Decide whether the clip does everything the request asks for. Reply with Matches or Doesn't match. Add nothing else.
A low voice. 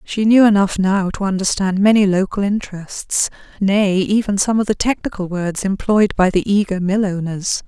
Doesn't match